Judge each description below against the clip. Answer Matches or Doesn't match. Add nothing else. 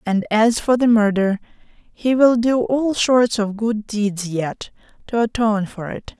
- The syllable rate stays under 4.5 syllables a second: Matches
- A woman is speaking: Matches